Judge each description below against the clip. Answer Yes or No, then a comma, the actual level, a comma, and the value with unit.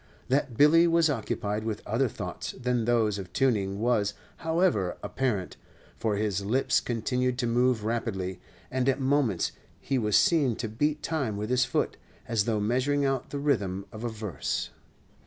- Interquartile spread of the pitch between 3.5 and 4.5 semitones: Yes, average, 4.1 semitones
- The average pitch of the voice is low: Yes, low, 120 Hz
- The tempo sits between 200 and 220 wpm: No, average, 165 wpm